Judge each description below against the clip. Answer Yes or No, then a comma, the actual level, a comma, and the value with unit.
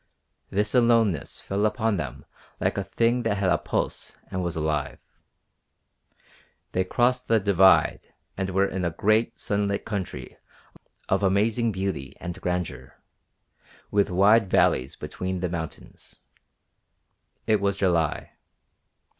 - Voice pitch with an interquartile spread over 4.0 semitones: No, average, 3.3 semitones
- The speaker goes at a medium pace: No, slow, 125 wpm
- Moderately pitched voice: No, very low, 95 Hz